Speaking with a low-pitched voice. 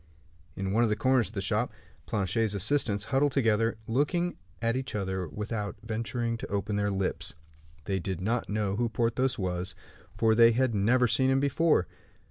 Yes: low, 110 Hz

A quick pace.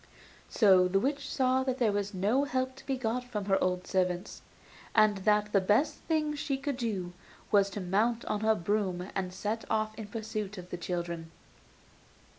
No: average, 180 wpm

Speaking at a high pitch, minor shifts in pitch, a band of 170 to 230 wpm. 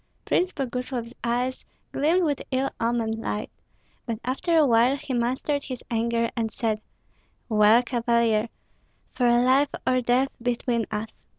No: high, 245 Hz; narrow, 2.3 semitones; slow, 135 wpm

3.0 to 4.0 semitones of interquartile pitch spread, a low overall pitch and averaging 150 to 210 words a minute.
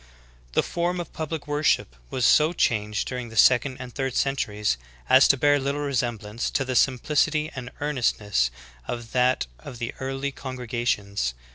Yes: average, 3.6 semitones; low, 130 Hz; average, 160 wpm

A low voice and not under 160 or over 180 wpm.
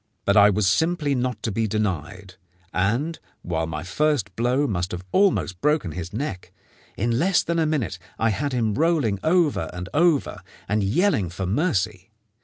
Yes: low, 110 Hz; average, 170 wpm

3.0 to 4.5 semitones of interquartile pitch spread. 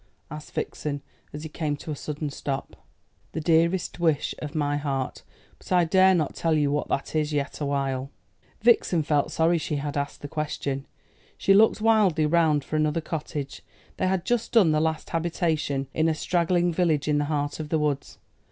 No: narrow, 2.6 semitones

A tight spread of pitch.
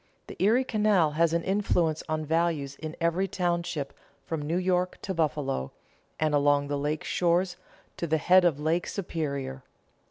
No: average, 3.2 semitones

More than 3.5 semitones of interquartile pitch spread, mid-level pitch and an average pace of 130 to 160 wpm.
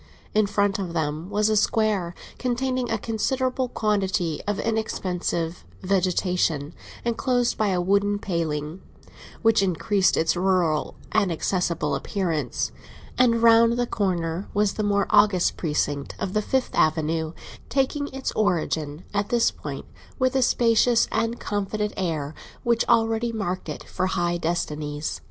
No: average, 4.9 semitones; high, 200 Hz; average, 140 wpm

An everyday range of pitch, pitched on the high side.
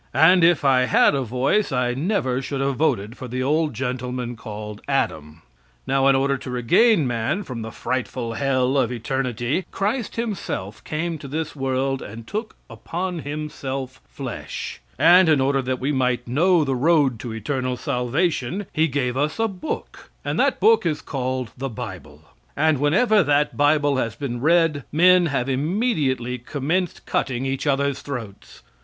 No: average, 4.1 semitones; low, 135 Hz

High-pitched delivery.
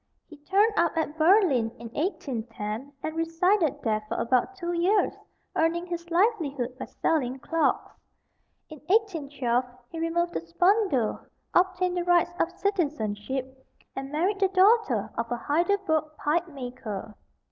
Yes: very high, 320 Hz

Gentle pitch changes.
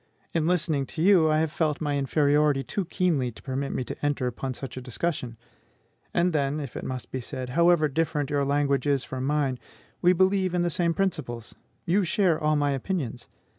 No: average, 3.9 semitones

